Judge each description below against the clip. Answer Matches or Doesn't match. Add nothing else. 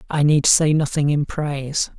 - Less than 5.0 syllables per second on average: Matches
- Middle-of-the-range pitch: Matches